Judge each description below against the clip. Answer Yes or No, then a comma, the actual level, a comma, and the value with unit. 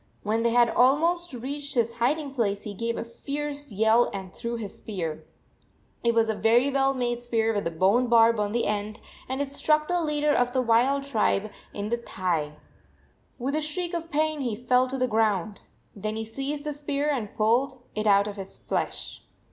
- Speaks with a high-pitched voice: Yes, high, 235 Hz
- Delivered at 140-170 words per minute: No, fast, 205 wpm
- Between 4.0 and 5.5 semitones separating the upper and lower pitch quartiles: Yes, average, 4.5 semitones